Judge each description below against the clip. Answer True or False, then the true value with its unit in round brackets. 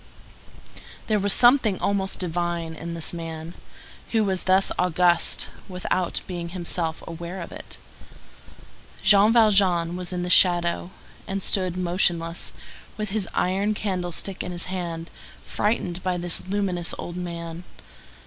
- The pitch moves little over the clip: True (2.1 semitones)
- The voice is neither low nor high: True (180 Hz)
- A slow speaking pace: True (130 wpm)